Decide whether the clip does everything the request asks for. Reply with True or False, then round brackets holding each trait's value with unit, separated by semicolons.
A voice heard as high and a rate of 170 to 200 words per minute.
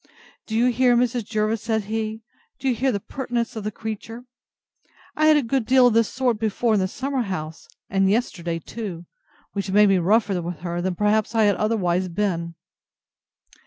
True (215 Hz; 190 wpm)